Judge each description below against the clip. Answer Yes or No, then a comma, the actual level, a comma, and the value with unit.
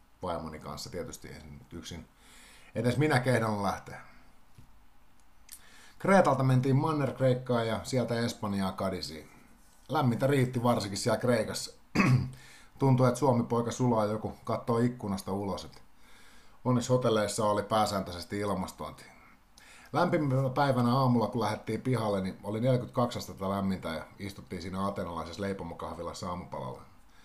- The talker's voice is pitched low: Yes, low, 110 Hz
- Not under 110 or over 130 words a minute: Yes, average, 115 wpm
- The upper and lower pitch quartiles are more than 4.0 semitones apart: Yes, average, 4.8 semitones